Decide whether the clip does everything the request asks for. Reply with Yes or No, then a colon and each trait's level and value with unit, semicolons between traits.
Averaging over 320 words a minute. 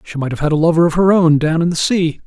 Yes: fast, 345 wpm